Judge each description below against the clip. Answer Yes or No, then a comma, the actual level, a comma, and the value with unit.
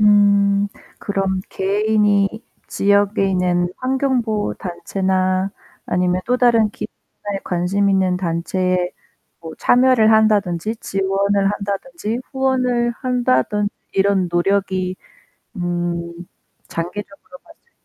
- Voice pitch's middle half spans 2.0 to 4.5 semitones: Yes, average, 2.9 semitones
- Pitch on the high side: Yes, high, 200 Hz